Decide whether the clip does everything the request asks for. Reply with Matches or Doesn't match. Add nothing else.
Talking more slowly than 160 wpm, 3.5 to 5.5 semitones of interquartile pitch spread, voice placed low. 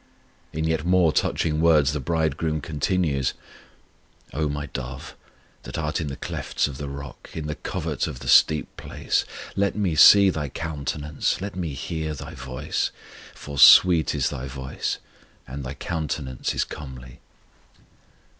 Doesn't match